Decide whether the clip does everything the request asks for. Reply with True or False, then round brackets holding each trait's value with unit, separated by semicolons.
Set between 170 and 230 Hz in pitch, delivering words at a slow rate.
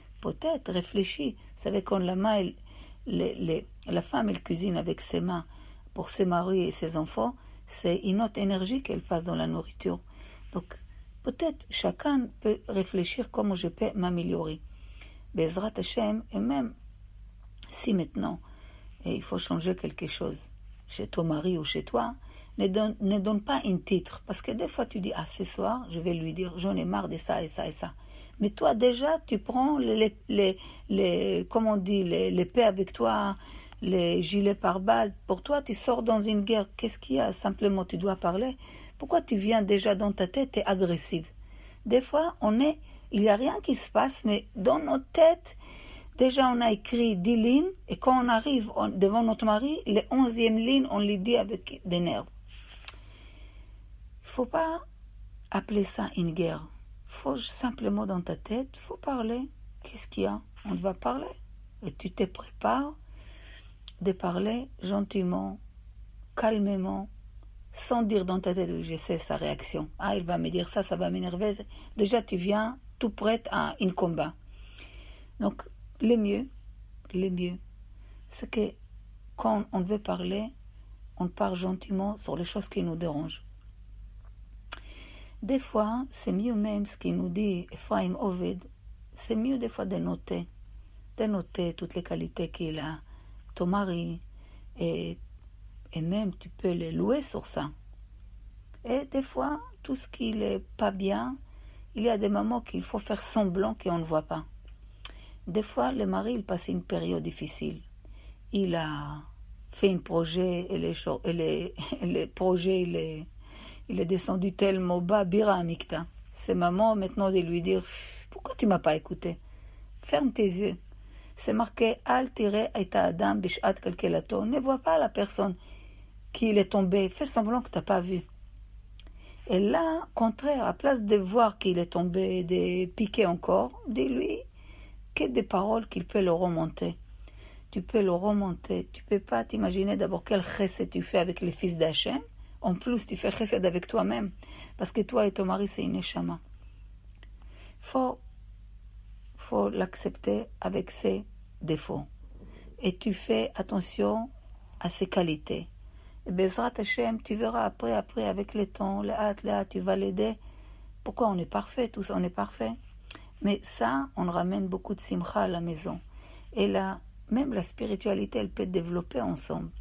False (185 Hz; 165 wpm)